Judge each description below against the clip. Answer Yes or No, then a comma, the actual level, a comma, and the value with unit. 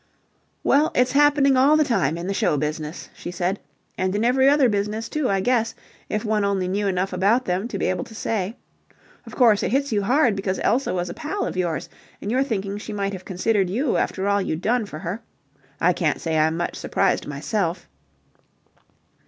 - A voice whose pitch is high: Yes, high, 200 Hz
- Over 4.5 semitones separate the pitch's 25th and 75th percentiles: Yes, average, 5.1 semitones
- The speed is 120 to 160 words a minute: No, fast, 205 wpm